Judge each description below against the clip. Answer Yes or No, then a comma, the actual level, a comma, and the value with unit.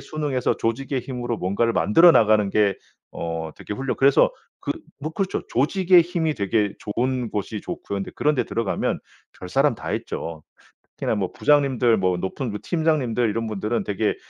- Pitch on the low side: Yes, low, 115 Hz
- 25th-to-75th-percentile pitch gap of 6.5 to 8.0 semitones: No, average, 5.3 semitones